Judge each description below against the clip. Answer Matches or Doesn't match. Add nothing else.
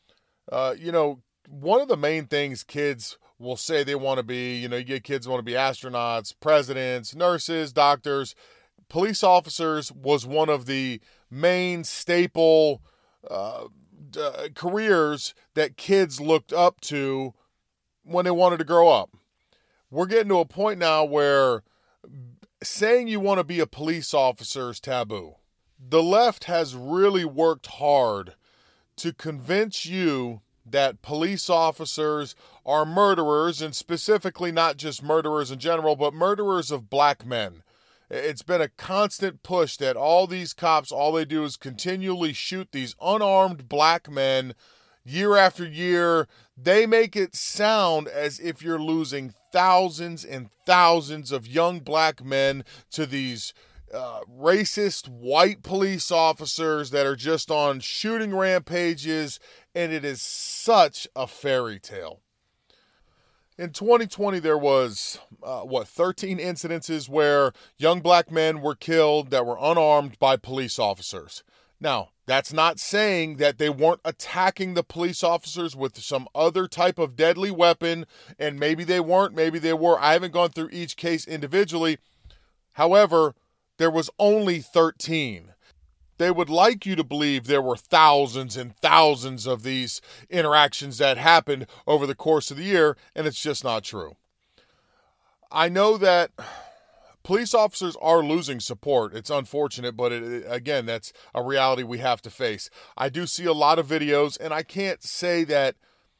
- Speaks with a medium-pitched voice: Matches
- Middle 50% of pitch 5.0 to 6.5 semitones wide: Doesn't match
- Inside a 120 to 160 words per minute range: Matches